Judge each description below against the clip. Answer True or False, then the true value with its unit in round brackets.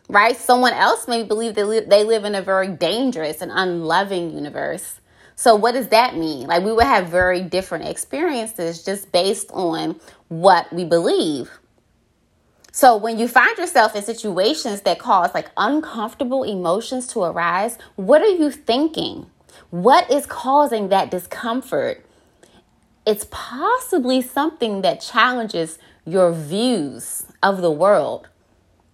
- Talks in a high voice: True (205 Hz)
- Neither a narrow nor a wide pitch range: False (6.2 semitones)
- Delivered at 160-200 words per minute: False (140 wpm)